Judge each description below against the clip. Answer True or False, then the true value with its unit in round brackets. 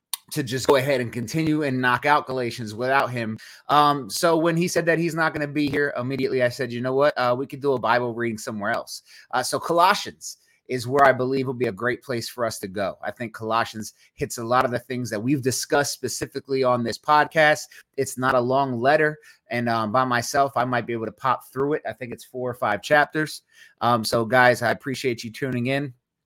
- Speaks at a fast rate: True (235 wpm)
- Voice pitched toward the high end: False (130 Hz)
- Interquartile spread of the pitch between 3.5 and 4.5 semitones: False (3.1 semitones)